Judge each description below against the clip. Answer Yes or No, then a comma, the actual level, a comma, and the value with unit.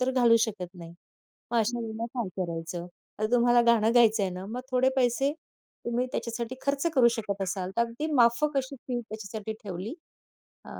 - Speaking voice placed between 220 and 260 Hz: Yes, high, 230 Hz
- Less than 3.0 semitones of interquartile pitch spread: No, average, 3.6 semitones